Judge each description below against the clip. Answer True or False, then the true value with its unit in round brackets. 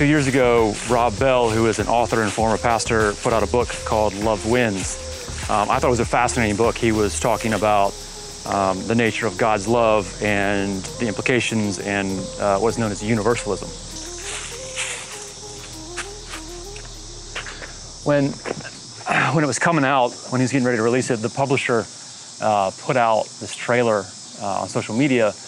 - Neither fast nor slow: True (165 wpm)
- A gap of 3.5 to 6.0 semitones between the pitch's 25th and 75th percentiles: False (2.8 semitones)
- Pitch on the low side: True (115 Hz)